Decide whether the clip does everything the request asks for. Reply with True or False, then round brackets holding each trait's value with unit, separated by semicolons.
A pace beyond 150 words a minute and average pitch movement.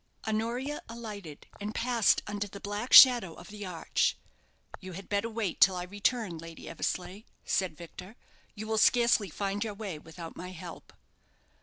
True (160 wpm; 3.5 semitones)